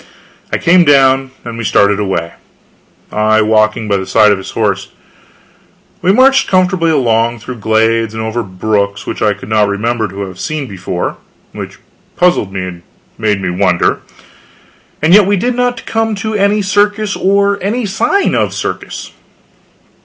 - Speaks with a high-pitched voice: No, low, 115 Hz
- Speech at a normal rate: Yes, average, 160 wpm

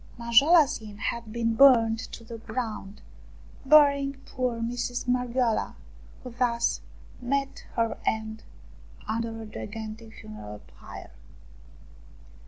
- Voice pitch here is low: No, high, 230 Hz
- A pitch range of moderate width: No, narrow, 2.2 semitones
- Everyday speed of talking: No, slow, 105 wpm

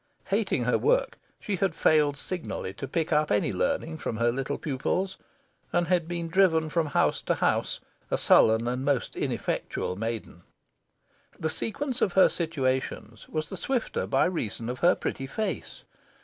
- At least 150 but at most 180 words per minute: Yes, average, 165 wpm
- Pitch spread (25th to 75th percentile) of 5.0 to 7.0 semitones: Yes, wide, 5.6 semitones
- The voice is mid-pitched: Yes, medium, 155 Hz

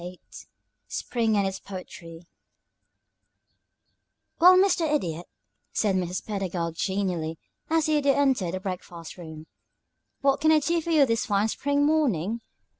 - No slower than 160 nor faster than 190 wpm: No, slow, 135 wpm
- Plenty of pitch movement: Yes, wide, 8.3 semitones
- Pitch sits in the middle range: No, high, 205 Hz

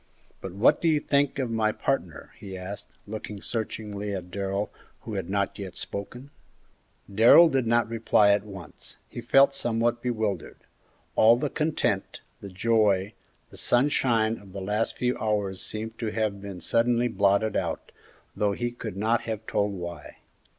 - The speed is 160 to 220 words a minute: Yes, average, 165 wpm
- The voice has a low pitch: Yes, low, 110 Hz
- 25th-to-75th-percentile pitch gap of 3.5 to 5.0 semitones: No, average, 3.0 semitones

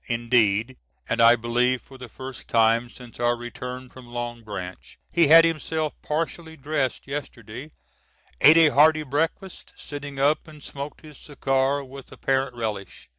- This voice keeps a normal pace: Yes, average, 150 wpm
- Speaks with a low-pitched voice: Yes, low, 130 Hz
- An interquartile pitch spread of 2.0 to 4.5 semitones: Yes, average, 3.8 semitones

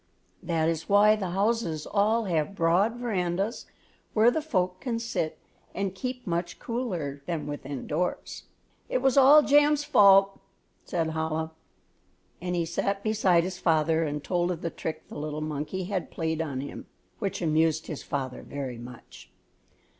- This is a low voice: No, medium, 175 Hz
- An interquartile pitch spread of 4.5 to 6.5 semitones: Yes, average, 4.9 semitones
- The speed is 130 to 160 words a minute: Yes, average, 155 wpm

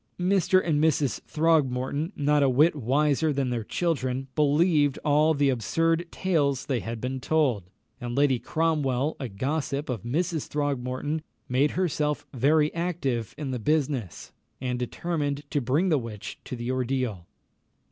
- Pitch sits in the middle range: Yes, medium, 145 Hz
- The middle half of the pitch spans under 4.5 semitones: Yes, average, 3.6 semitones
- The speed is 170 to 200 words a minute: No, average, 145 wpm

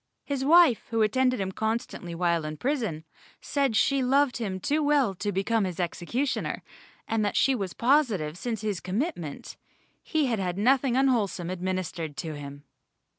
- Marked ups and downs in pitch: Yes, wide, 6.6 semitones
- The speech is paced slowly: No, average, 160 wpm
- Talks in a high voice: Yes, high, 215 Hz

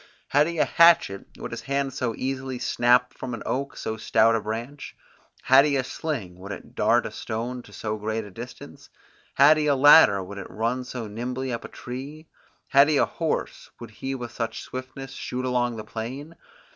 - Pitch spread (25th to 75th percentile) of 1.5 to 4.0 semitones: Yes, average, 3.3 semitones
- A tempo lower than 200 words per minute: No, fast, 205 wpm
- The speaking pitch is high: No, low, 125 Hz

